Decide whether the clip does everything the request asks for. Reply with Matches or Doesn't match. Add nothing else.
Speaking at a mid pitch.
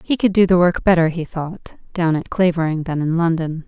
Matches